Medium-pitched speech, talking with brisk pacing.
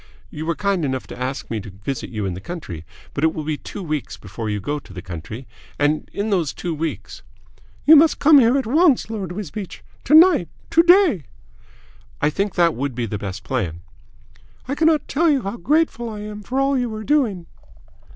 Yes: medium, 175 Hz; fast, 210 wpm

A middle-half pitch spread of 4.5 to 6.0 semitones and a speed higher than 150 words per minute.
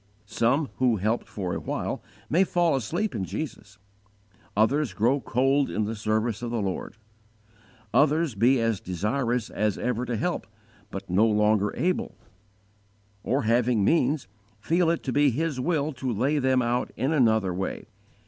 Yes: average, 4.9 semitones; average, 160 wpm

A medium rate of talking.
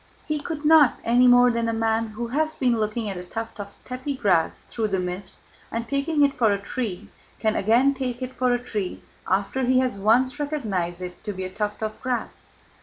No: fast, 215 wpm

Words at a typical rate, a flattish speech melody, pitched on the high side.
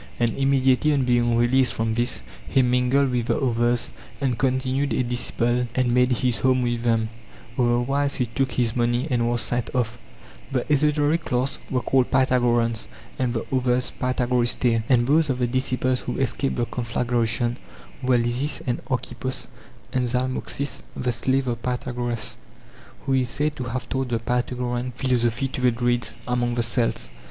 No: average, 170 wpm; narrow, 1.5 semitones; low, 125 Hz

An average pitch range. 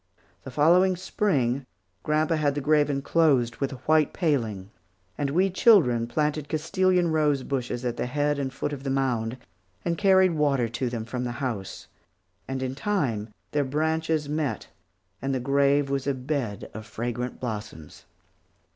Yes: average, 4.0 semitones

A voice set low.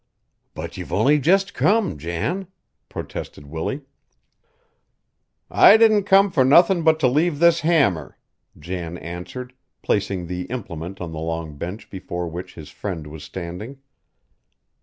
Yes: low, 100 Hz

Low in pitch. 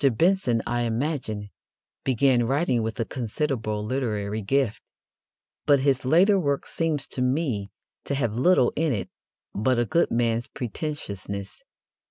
Yes: low, 125 Hz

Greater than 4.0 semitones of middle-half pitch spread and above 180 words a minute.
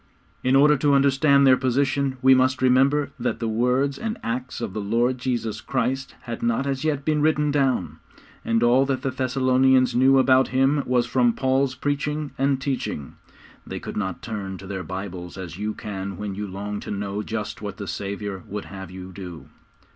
Yes: average, 4.8 semitones; average, 190 wpm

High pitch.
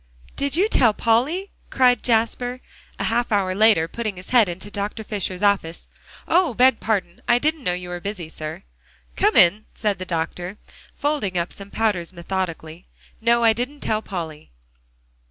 Yes: high, 210 Hz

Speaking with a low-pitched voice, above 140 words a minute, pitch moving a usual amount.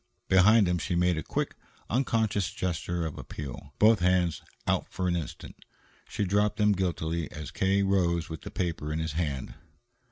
Yes: very low, 90 Hz; average, 170 wpm; average, 3.5 semitones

